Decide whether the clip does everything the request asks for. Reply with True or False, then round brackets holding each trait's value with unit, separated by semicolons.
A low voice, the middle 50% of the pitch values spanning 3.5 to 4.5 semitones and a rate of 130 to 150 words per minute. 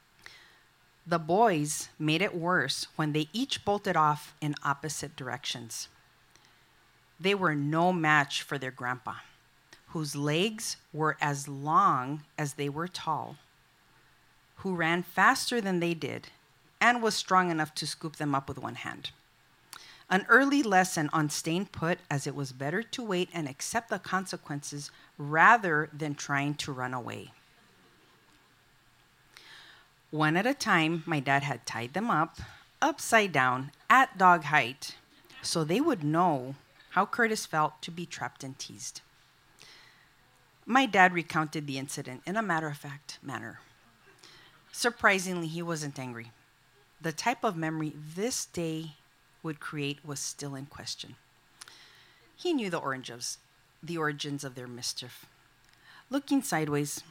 False (155 Hz; 4.1 semitones; 140 wpm)